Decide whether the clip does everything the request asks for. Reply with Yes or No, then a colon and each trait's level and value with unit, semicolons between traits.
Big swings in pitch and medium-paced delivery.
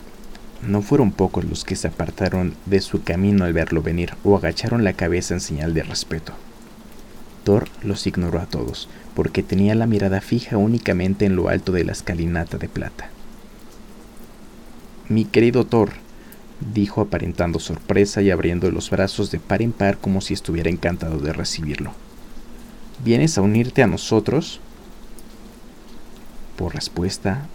No: average, 3.3 semitones; average, 145 wpm